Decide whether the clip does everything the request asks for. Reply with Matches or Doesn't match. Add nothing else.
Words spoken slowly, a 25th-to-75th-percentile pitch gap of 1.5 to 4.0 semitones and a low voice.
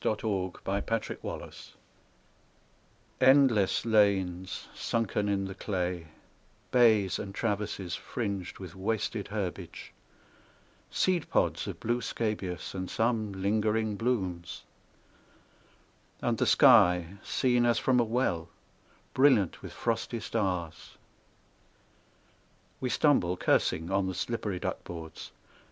Matches